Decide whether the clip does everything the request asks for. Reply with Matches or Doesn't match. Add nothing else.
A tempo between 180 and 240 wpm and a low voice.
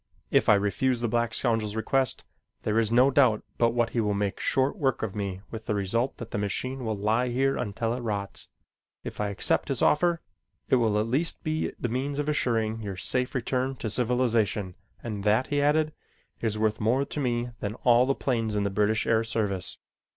Matches